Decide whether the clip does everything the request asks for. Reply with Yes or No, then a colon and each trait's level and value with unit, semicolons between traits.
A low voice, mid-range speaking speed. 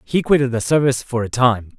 No: low, 125 Hz; fast, 235 wpm